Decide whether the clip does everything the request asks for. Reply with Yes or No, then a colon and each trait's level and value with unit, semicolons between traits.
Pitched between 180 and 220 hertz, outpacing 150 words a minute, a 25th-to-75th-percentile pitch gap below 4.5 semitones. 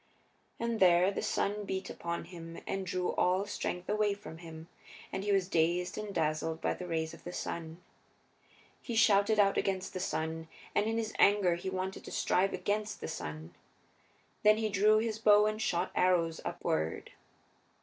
Yes: high, 190 Hz; average, 175 wpm; average, 3.5 semitones